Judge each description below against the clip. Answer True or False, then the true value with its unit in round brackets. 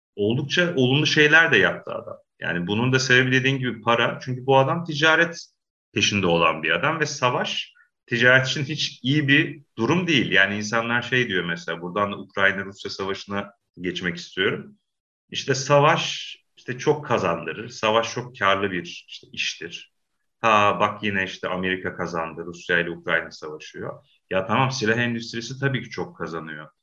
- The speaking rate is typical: False (155 wpm)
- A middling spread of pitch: False (6.0 semitones)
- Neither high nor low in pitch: False (115 Hz)